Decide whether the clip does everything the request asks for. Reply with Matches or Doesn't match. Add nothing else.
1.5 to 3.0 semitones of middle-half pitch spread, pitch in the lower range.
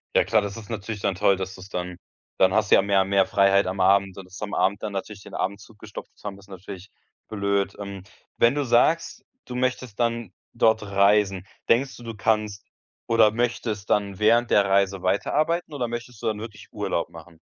Matches